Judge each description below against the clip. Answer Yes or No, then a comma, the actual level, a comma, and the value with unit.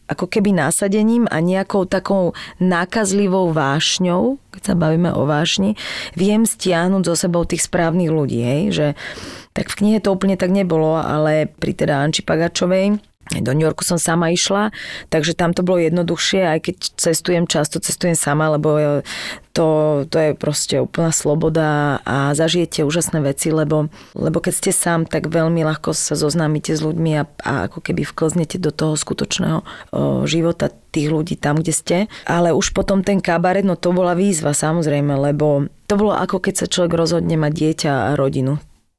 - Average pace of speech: No, fast, 170 wpm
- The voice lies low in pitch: No, medium, 165 Hz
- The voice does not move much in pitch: No, average, 3.2 semitones